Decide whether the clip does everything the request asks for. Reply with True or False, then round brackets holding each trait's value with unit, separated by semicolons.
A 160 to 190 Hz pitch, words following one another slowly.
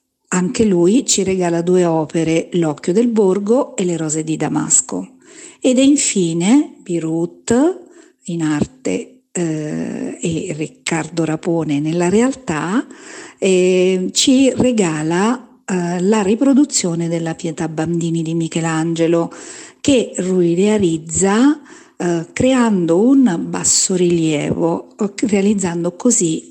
True (185 Hz; 105 wpm)